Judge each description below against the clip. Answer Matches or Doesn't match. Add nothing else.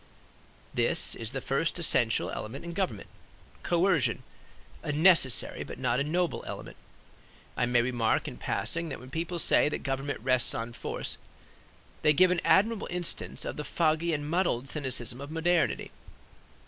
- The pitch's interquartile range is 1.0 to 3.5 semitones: Doesn't match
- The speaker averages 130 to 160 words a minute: Matches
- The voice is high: Doesn't match